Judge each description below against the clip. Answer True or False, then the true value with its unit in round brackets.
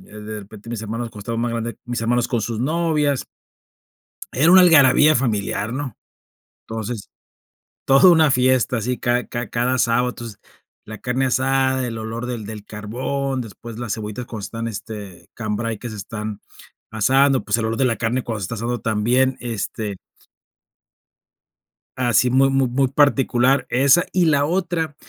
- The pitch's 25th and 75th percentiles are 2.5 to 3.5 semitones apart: True (3.1 semitones)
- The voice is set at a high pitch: False (120 Hz)